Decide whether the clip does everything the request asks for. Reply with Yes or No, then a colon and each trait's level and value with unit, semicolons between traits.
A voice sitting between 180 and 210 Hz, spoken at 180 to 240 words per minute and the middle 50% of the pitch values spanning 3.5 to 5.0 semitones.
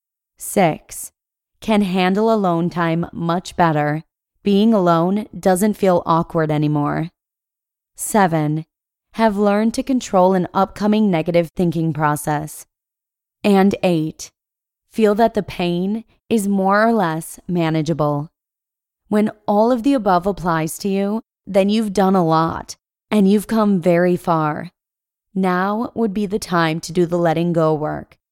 No: medium, 185 Hz; slow, 135 wpm; average, 4.1 semitones